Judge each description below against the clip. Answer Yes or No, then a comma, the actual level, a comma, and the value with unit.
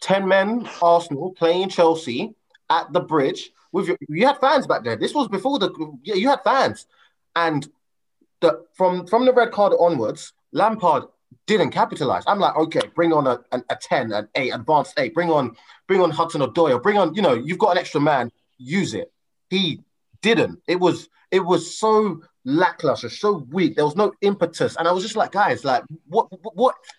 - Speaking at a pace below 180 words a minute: No, average, 195 wpm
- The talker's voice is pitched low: No, medium, 180 Hz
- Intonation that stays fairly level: No, average, 4.3 semitones